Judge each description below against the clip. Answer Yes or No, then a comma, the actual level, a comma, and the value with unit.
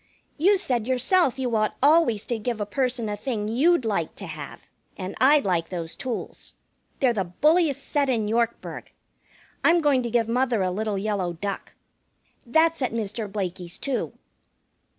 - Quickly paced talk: No, average, 165 wpm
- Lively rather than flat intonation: No, average, 4.8 semitones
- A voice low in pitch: No, high, 230 Hz